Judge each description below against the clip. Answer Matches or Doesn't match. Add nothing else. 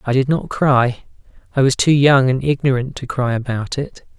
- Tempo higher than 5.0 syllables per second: Doesn't match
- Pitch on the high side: Doesn't match